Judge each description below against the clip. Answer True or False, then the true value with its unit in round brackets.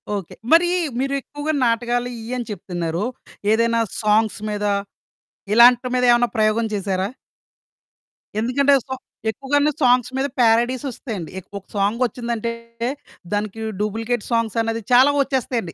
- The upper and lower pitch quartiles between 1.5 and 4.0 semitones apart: True (2.9 semitones)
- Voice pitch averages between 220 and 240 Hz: True (230 Hz)